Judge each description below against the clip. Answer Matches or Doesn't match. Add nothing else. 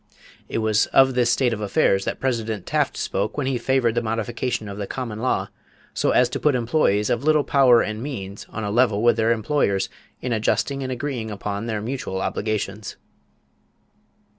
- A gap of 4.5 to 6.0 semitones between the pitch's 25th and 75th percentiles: Doesn't match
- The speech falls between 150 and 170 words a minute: Doesn't match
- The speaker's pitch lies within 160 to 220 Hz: Doesn't match